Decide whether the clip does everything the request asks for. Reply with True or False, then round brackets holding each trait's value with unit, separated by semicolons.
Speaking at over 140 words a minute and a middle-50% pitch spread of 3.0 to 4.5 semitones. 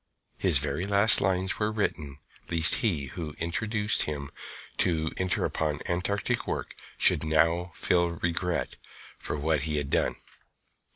False (135 wpm; 3.5 semitones)